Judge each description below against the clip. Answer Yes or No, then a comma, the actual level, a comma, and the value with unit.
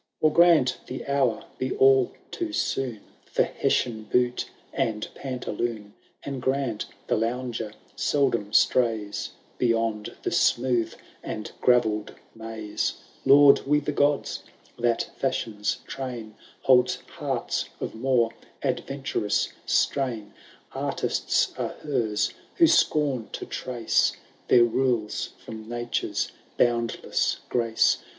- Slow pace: Yes, slow, 110 wpm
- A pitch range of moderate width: Yes, average, 3.1 semitones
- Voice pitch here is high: No, low, 120 Hz